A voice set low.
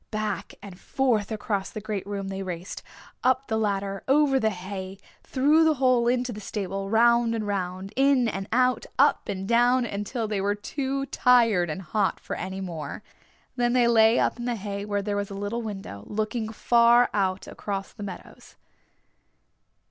No: high, 215 Hz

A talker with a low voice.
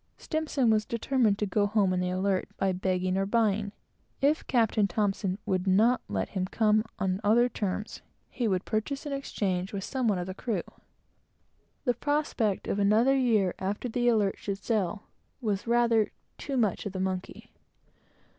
No: high, 210 Hz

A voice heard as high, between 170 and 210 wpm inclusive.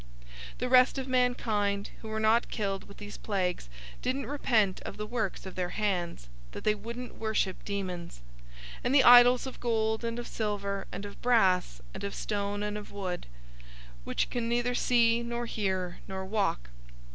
Yes: high, 210 Hz; average, 175 wpm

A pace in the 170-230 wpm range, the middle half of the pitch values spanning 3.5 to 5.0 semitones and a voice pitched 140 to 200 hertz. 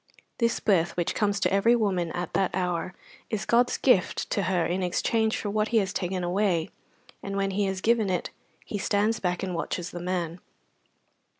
No: average, 190 wpm; average, 3.0 semitones; high, 190 Hz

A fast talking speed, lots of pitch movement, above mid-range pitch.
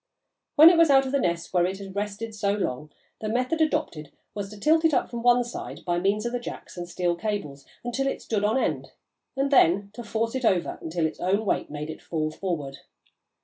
Yes: fast, 230 wpm; wide, 5.9 semitones; high, 205 Hz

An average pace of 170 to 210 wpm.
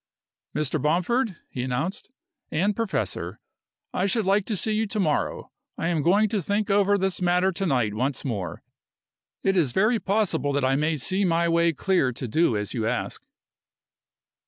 Yes: average, 175 wpm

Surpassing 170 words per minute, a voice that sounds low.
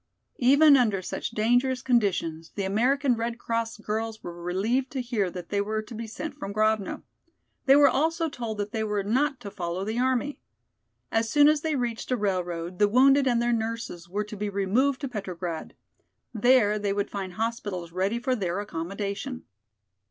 No: average, 180 wpm; high, 220 Hz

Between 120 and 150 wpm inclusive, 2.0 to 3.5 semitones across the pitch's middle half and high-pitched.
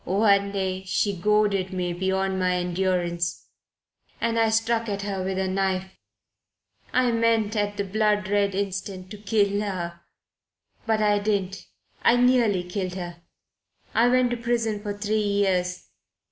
Yes: average, 145 wpm; narrow, 2.4 semitones; high, 200 Hz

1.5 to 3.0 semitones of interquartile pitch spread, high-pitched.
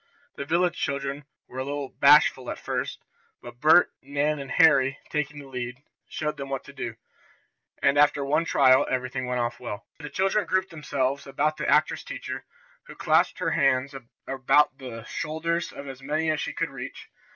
No: narrow, 2.5 semitones; medium, 140 Hz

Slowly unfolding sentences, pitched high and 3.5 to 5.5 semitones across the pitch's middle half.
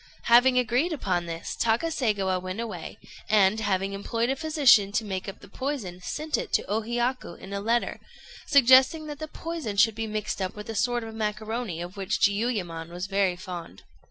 No: average, 185 wpm; high, 215 Hz; average, 4.4 semitones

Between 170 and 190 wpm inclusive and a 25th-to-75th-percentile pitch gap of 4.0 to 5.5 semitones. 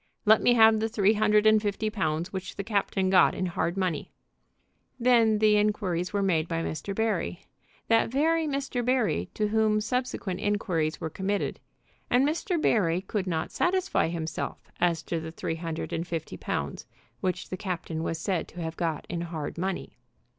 Yes: average, 175 wpm; average, 4.6 semitones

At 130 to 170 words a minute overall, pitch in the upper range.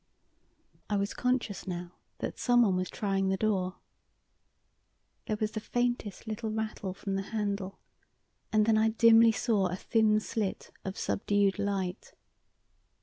Yes: average, 140 wpm; high, 210 Hz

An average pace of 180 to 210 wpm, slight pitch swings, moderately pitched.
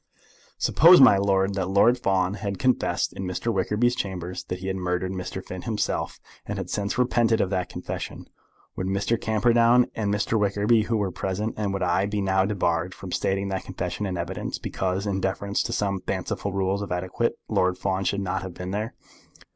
No: average, 195 wpm; narrow, 2.0 semitones; low, 100 Hz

